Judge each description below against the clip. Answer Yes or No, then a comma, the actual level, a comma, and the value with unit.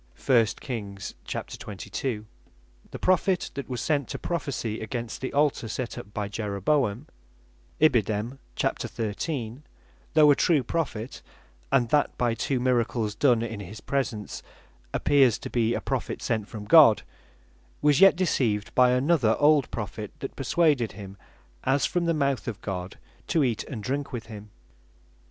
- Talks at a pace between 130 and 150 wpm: Yes, average, 140 wpm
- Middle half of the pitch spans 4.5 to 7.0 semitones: Yes, average, 4.8 semitones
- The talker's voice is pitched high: No, low, 120 Hz